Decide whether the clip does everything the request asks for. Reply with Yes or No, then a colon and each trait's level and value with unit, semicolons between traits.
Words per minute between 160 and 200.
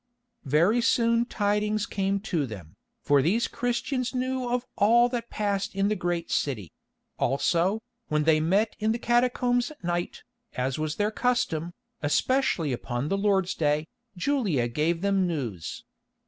No: average, 145 wpm